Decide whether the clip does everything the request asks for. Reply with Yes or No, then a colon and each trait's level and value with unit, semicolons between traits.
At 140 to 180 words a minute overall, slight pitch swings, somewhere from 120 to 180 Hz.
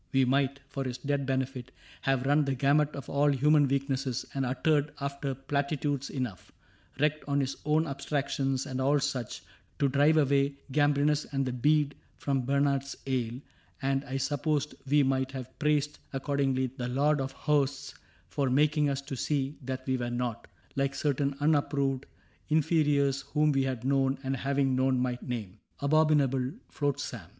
Yes: average, 165 wpm; narrow, 1.6 semitones; medium, 140 Hz